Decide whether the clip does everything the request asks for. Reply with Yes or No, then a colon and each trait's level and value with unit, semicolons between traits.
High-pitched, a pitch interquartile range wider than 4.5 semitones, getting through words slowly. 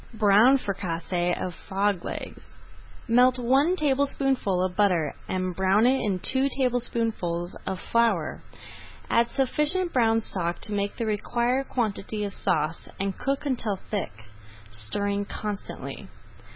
Yes: high, 210 Hz; average, 5.1 semitones; slow, 125 wpm